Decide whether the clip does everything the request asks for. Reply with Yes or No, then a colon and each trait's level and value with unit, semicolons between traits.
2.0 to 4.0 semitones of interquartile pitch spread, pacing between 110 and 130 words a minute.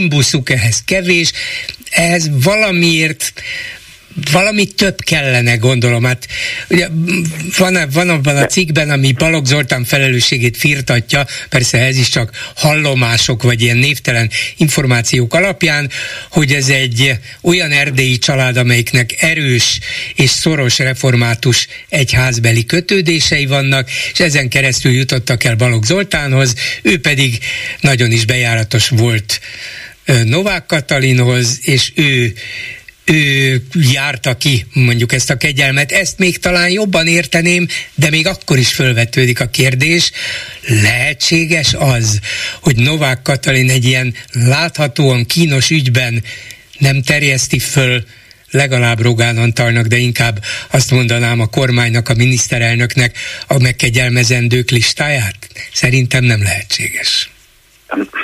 No: average, 4.5 semitones; average, 115 wpm